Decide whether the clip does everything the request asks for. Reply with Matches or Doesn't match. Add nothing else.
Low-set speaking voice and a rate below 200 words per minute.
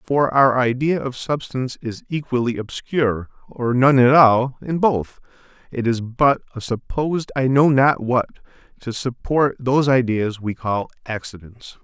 Matches